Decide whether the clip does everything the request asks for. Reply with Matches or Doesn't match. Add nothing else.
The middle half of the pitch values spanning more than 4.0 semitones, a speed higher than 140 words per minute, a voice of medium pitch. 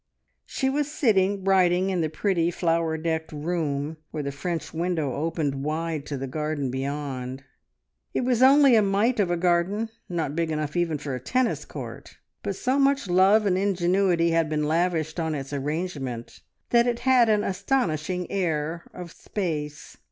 Matches